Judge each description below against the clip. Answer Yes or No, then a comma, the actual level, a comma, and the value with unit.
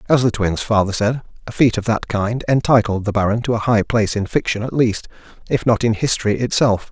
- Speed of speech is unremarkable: No, fast, 225 wpm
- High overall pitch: No, low, 110 Hz